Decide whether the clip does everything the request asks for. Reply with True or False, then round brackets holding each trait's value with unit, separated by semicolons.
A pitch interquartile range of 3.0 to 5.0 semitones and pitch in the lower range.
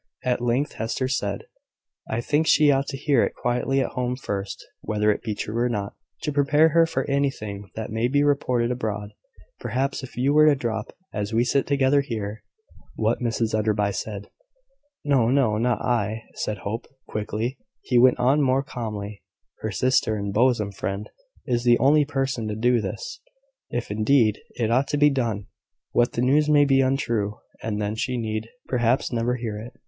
True (4.0 semitones; 120 Hz)